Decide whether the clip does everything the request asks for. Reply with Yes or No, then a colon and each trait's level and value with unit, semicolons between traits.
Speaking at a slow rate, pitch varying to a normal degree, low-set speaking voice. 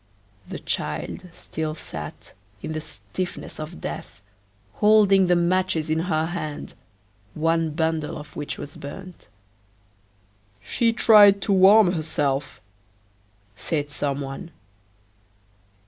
No: slow, 105 wpm; average, 3.5 semitones; medium, 165 Hz